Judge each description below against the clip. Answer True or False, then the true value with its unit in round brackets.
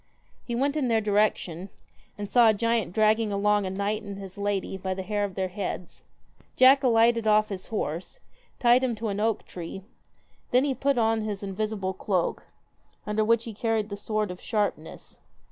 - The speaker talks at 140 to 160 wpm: False (185 wpm)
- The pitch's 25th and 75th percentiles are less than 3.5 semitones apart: True (2.5 semitones)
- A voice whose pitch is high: True (210 Hz)